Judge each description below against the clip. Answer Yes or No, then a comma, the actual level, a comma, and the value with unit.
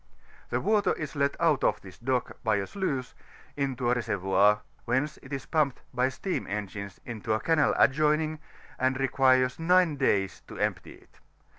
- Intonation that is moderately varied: No, wide, 5.7 semitones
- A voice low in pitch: Yes, low, 130 Hz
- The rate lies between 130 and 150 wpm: No, average, 170 wpm